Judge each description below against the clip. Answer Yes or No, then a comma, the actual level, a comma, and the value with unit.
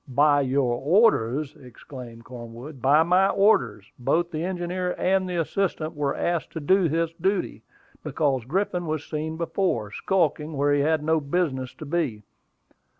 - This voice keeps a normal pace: Yes, average, 150 wpm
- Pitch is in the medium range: Yes, medium, 155 Hz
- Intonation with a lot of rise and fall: No, average, 4.7 semitones